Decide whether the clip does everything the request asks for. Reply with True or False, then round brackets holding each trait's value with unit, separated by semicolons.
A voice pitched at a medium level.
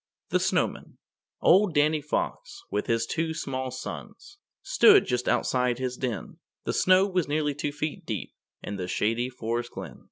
True (145 Hz)